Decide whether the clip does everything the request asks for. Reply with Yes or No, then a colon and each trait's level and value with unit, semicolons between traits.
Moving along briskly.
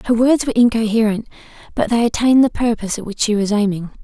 Yes: fast, 210 wpm